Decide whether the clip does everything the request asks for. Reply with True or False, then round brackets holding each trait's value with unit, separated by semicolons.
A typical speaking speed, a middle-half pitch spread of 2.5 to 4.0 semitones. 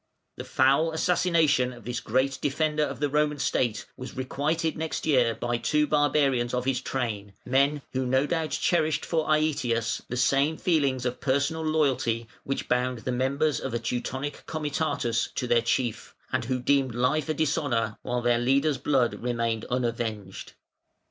True (160 wpm; 3.7 semitones)